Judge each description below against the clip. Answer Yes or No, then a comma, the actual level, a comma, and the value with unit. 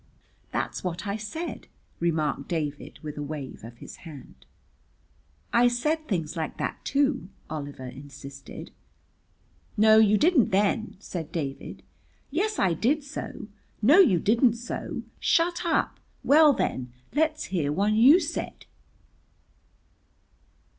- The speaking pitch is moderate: No, high, 205 Hz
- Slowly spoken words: Yes, slow, 125 wpm